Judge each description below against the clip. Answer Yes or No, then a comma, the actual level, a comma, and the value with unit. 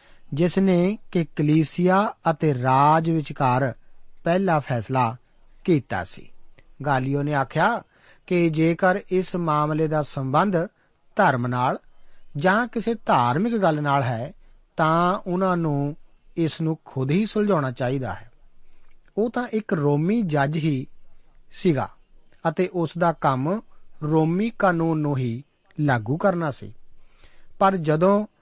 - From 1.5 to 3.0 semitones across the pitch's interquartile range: No, average, 5.1 semitones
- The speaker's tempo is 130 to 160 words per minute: No, average, 120 wpm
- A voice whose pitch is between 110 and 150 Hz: No, medium, 160 Hz